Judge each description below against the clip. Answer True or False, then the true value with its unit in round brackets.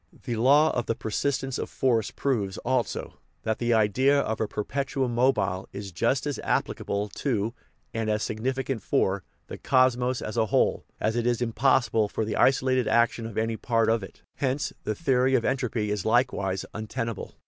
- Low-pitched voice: True (115 Hz)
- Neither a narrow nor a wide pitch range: True (3.2 semitones)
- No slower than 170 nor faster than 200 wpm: True (180 wpm)